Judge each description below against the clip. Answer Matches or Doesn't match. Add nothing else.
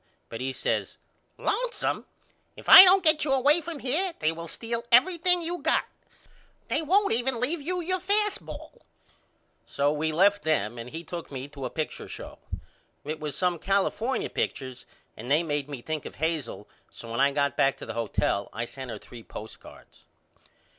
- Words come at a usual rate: Matches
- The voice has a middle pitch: Matches